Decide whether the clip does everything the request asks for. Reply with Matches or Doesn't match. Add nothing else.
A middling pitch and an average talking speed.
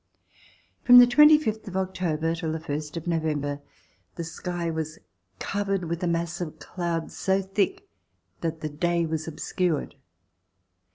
Matches